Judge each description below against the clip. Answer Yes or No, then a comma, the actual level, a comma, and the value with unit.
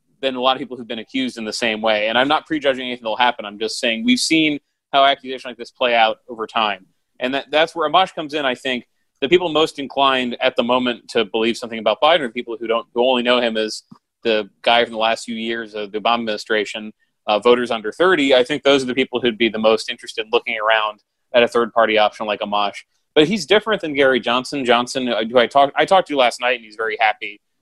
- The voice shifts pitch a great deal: No, average, 3.4 semitones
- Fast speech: Yes, fast, 255 wpm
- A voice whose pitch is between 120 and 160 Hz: Yes, low, 125 Hz